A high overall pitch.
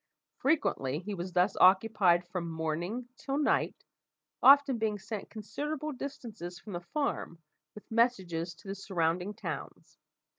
Yes: high, 200 Hz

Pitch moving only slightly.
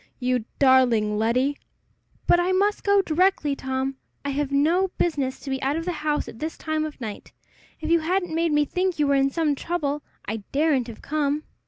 No: average, 3.7 semitones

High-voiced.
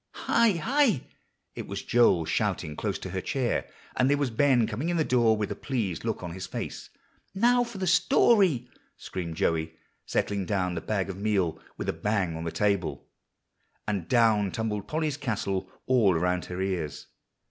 No: low, 105 Hz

